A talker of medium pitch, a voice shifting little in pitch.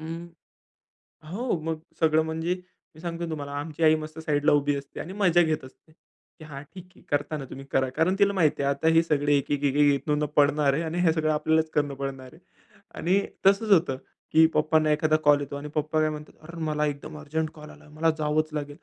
Yes: medium, 155 Hz; narrow, 1.9 semitones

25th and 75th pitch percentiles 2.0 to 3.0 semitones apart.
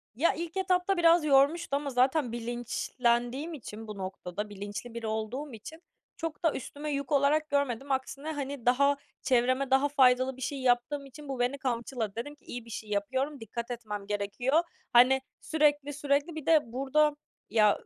No: average, 3.7 semitones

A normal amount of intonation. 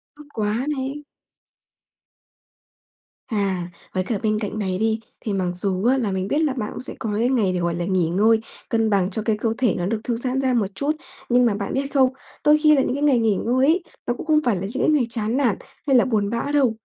Yes: average, 4.6 semitones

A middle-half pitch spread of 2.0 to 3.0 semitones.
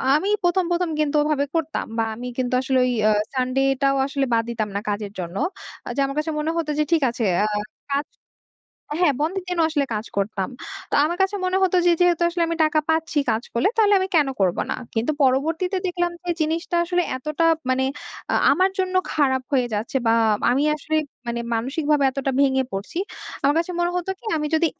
No: average, 4.9 semitones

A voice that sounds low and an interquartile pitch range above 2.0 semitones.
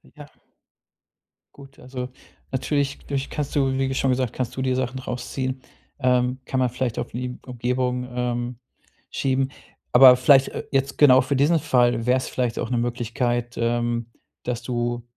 No: low, 125 Hz; narrow, 1.6 semitones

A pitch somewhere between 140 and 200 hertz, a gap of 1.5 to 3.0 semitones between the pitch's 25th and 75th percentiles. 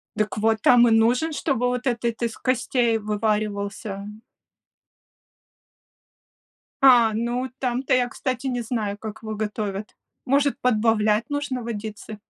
No: high, 230 Hz; average, 2.7 semitones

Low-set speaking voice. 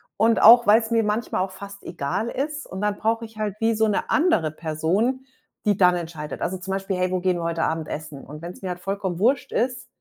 No: high, 195 Hz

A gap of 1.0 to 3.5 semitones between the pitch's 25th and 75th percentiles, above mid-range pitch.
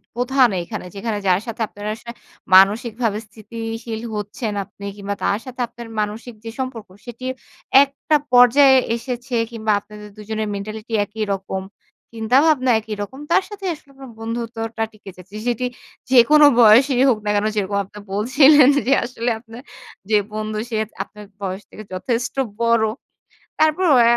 Yes: average, 3.2 semitones; high, 230 Hz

